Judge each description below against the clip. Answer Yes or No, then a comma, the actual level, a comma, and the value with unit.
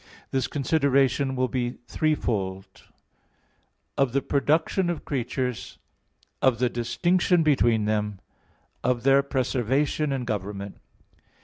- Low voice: Yes, low, 130 Hz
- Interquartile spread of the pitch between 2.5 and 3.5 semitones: Yes, average, 3.2 semitones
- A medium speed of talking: No, slow, 120 wpm